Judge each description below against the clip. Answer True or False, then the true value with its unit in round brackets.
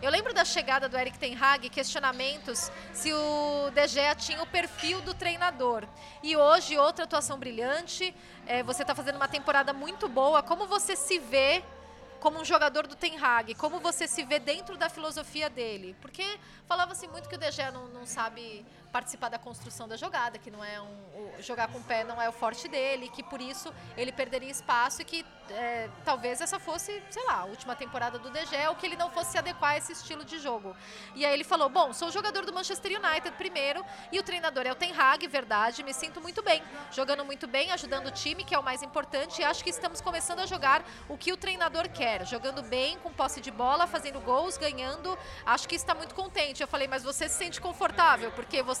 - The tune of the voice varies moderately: True (4.5 semitones)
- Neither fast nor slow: False (220 wpm)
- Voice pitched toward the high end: True (295 Hz)